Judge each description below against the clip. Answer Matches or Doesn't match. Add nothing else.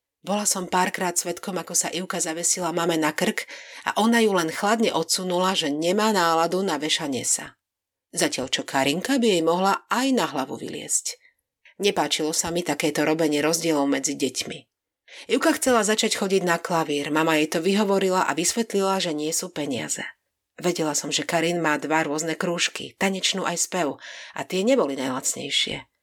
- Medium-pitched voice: Matches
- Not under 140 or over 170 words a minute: Matches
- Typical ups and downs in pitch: Matches